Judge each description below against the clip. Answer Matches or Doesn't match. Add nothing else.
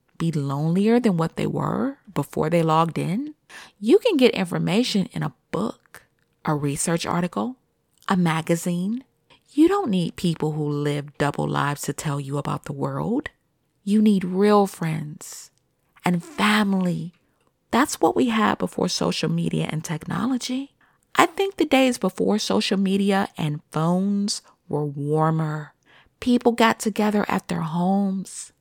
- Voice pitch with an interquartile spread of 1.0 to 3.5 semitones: Doesn't match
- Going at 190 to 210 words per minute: Doesn't match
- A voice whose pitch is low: Doesn't match